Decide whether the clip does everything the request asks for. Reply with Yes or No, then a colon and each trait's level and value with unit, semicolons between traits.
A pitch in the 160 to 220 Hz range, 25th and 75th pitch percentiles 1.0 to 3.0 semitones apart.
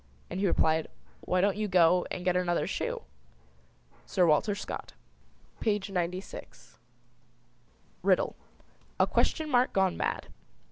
Yes: medium, 185 Hz; narrow, 2.4 semitones